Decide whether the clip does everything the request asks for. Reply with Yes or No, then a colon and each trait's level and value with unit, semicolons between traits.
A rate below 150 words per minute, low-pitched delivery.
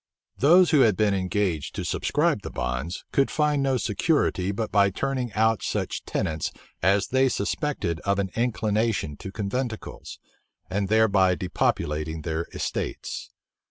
Yes: average, 140 wpm; low, 100 Hz